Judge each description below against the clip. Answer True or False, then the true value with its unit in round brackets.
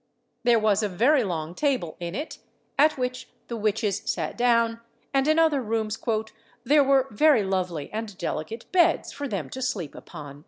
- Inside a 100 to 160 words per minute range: False (170 wpm)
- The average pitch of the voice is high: True (225 Hz)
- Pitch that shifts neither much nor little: False (5.9 semitones)